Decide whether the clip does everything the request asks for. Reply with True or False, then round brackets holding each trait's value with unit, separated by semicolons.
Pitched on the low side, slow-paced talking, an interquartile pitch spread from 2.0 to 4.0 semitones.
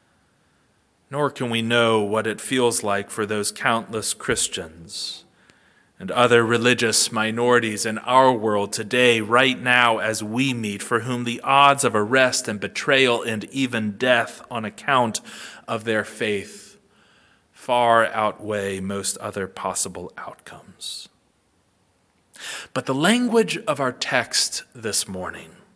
True (115 Hz; 130 wpm; 2.9 semitones)